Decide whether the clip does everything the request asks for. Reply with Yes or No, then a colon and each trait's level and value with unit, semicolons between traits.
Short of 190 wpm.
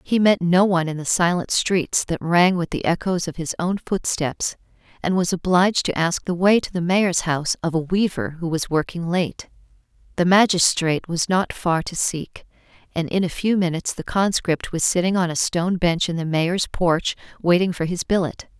No: fast, 205 wpm